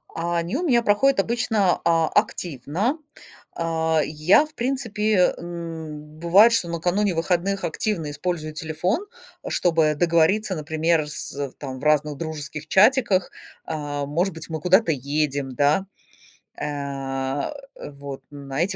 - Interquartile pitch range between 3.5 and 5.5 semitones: Yes, average, 4.4 semitones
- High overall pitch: No, medium, 165 Hz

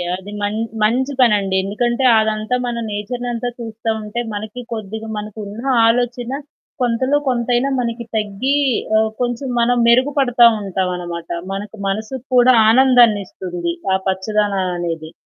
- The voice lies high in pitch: Yes, high, 220 Hz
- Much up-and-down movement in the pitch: No, average, 3.2 semitones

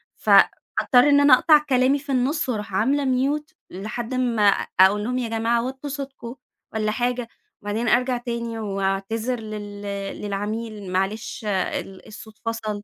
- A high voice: Yes, high, 230 Hz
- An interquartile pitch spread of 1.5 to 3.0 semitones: No, average, 3.5 semitones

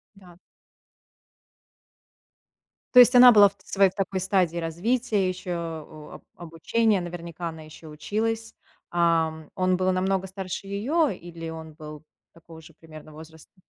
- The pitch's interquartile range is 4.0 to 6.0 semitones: No, average, 3.4 semitones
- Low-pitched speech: No, medium, 175 Hz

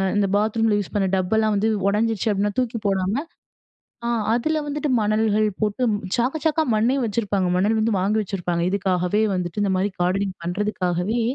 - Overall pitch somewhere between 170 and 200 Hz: No, high, 210 Hz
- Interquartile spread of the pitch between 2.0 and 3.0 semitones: Yes, average, 2.7 semitones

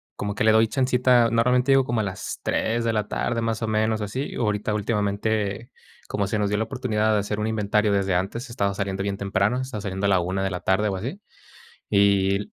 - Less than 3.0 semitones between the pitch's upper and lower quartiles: Yes, narrow, 2.5 semitones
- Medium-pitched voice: No, low, 105 Hz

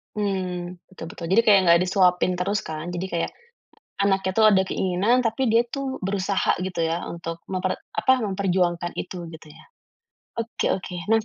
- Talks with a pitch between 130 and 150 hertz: No, high, 190 Hz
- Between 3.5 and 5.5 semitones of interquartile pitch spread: No, average, 2.8 semitones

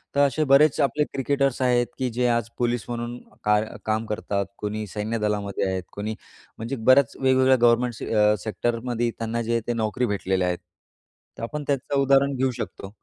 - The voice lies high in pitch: No, low, 120 Hz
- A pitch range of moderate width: Yes, average, 3.4 semitones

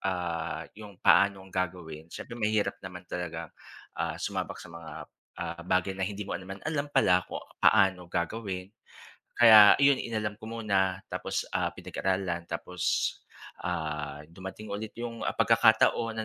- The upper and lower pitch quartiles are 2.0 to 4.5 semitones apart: Yes, average, 3.4 semitones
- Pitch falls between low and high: No, very low, 95 Hz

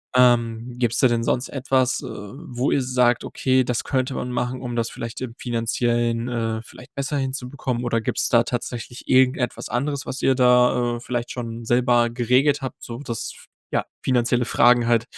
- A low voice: Yes, low, 125 Hz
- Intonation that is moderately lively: No, narrow, 1.5 semitones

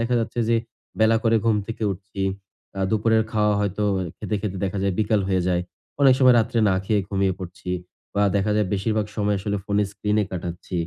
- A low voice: Yes, low, 105 Hz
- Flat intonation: Yes, narrow, 2.2 semitones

